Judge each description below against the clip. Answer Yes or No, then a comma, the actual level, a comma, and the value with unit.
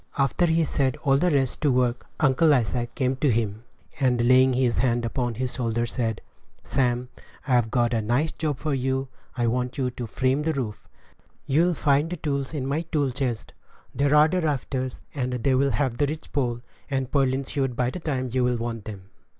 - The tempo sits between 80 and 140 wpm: No, average, 200 wpm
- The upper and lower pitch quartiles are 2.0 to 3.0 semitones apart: Yes, average, 2.7 semitones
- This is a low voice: Yes, low, 130 Hz